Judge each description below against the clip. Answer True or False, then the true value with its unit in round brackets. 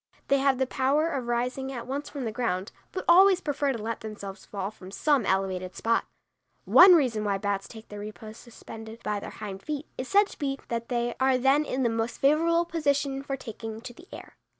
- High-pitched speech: True (245 Hz)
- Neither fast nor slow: False (215 wpm)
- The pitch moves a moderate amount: True (4.5 semitones)